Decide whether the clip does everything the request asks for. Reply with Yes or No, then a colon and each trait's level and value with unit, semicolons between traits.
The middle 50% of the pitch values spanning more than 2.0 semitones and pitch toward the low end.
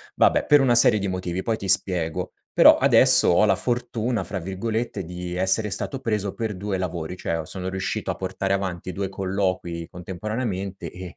Yes: average, 2.8 semitones; very low, 95 Hz